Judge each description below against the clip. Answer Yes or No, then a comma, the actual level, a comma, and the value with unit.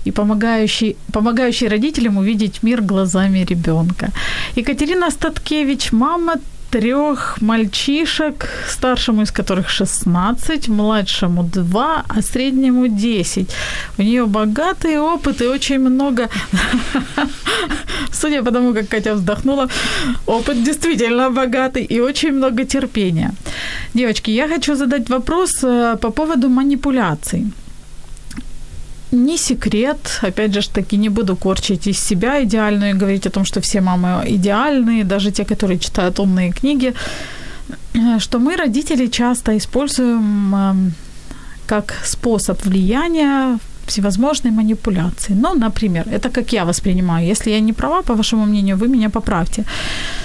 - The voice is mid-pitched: No, high, 225 Hz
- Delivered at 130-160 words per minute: No, average, 120 wpm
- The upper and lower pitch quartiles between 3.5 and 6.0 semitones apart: Yes, average, 4.4 semitones